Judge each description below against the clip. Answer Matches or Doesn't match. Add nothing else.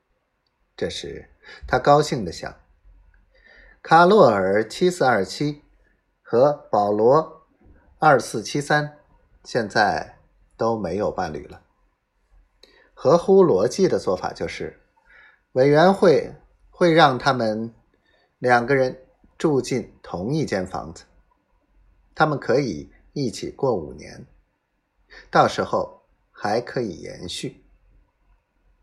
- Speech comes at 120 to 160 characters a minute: Matches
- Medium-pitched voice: Matches